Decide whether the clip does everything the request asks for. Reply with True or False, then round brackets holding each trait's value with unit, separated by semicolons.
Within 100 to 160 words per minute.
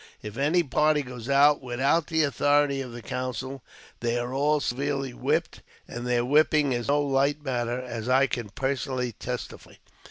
False (170 wpm)